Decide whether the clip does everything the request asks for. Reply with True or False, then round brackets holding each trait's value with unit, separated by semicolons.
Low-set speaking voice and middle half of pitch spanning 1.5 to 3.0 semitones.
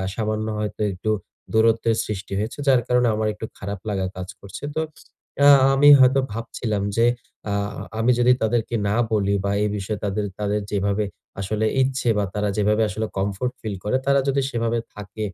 True (110 Hz; 2.4 semitones)